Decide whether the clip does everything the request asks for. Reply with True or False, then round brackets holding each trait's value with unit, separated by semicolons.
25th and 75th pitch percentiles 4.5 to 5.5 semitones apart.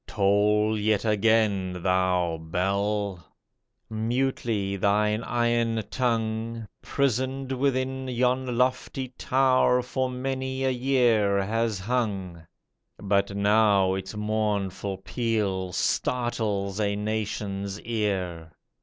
False (3.9 semitones)